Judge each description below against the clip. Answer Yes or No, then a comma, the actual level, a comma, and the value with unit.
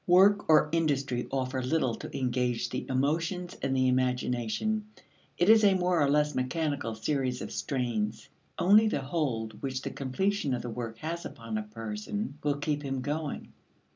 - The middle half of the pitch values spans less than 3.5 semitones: No, average, 4.7 semitones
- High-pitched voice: No, low, 135 Hz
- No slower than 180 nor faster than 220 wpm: No, average, 170 wpm